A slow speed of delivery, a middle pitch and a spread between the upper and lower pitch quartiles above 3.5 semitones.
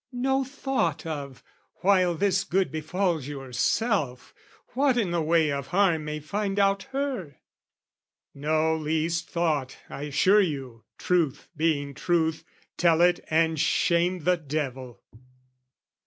Yes: slow, 125 wpm; medium, 165 Hz; average, 4.2 semitones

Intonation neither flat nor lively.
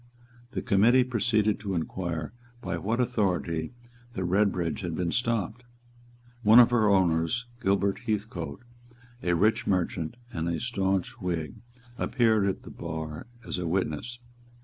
Yes: average, 4.9 semitones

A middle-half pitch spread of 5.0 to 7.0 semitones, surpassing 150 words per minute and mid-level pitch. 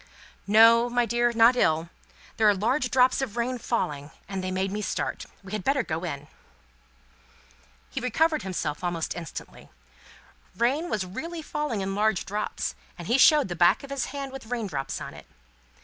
No: wide, 5.4 semitones; average, 180 wpm; high, 225 Hz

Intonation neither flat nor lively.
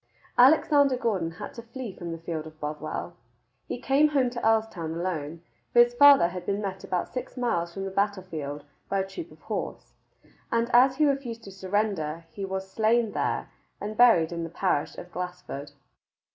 No: wide, 5.9 semitones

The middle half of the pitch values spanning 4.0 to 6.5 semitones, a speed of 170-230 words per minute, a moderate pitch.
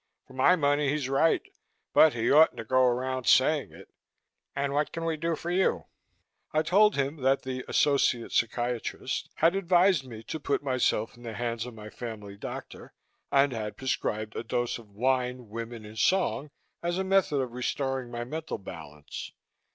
No: average, 4.5 semitones; average, 175 wpm; low, 130 Hz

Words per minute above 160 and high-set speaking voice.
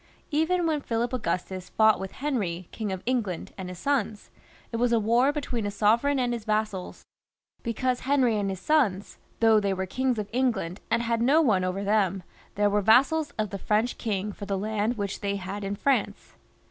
Yes: average, 200 wpm; high, 220 Hz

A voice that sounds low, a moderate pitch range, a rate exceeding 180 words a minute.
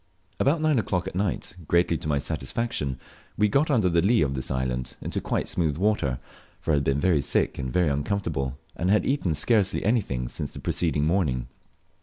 No: very low, 85 Hz; wide, 6.8 semitones; average, 190 wpm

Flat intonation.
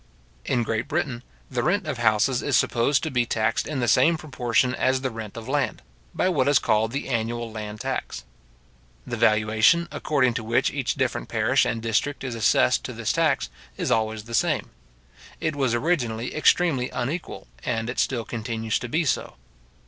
No: average, 3.9 semitones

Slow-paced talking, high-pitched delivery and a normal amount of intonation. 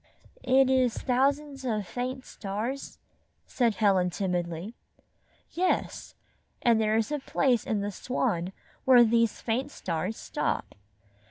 Yes: slow, 120 wpm; high, 230 Hz; average, 4.3 semitones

